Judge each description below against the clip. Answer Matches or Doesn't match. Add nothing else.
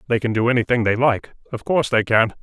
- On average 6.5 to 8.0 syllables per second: Matches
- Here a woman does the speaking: Doesn't match